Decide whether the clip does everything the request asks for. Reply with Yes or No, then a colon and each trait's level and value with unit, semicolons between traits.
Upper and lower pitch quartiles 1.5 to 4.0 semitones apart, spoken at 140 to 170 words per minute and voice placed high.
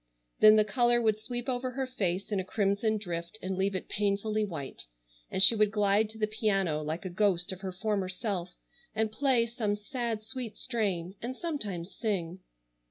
No: average, 3.1 semitones; average, 185 wpm; high, 210 Hz